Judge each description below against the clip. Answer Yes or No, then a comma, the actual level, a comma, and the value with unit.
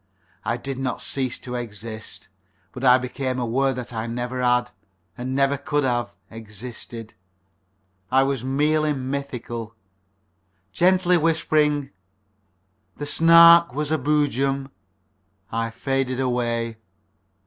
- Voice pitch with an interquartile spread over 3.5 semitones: No, average, 3.0 semitones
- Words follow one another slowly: Yes, slow, 115 wpm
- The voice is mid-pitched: No, low, 130 Hz